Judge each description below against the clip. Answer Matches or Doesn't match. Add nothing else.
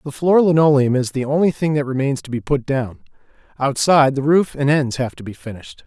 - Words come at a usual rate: Doesn't match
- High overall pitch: Doesn't match